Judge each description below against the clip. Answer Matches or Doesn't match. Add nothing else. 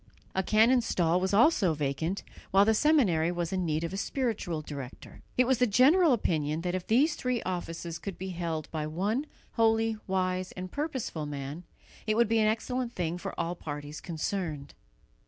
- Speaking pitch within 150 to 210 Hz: Matches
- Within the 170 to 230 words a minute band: Matches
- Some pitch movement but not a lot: Doesn't match